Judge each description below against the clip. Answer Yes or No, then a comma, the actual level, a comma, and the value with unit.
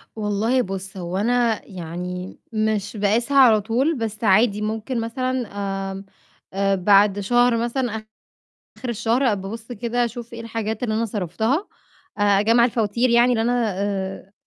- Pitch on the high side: Yes, high, 220 Hz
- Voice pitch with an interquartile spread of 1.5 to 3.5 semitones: Yes, average, 3.1 semitones